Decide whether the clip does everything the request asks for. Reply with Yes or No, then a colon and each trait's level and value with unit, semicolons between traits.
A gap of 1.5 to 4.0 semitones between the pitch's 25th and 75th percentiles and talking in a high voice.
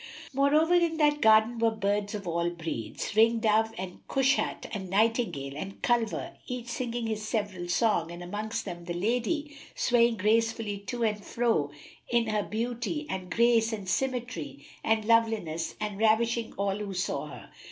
Yes: average, 3.3 semitones; high, 220 Hz